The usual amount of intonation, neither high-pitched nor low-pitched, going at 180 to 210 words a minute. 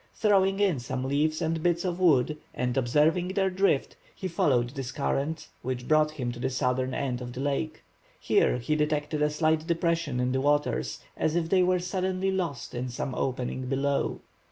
Yes: average, 4.8 semitones; medium, 150 Hz; average, 185 wpm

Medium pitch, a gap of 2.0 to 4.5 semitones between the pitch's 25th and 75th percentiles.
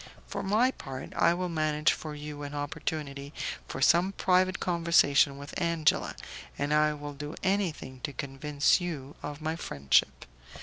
Yes: medium, 150 Hz; average, 3.0 semitones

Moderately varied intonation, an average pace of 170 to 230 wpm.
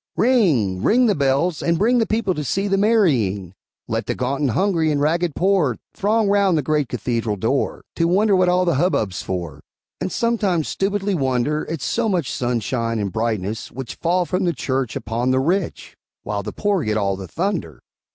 No: wide, 8.6 semitones; average, 190 wpm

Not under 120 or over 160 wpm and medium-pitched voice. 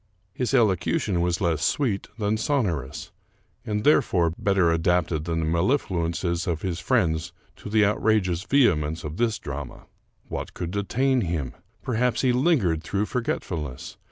No: average, 145 wpm; very low, 90 Hz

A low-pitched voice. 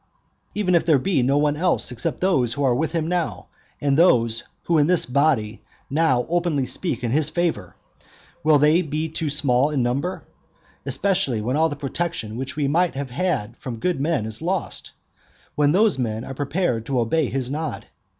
No: medium, 145 Hz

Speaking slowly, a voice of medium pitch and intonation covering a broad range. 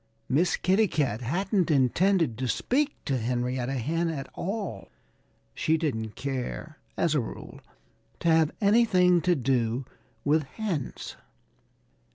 Yes: slow, 125 wpm; medium, 155 Hz; wide, 6.2 semitones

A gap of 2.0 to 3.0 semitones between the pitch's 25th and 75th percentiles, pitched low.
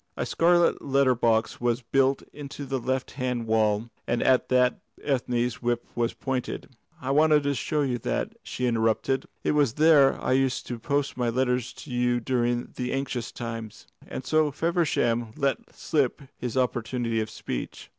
Yes: narrow, 2.6 semitones; low, 125 Hz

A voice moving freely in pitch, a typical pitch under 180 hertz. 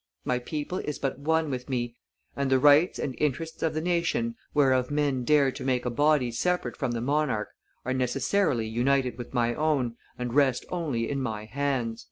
No: average, 3.5 semitones; low, 135 Hz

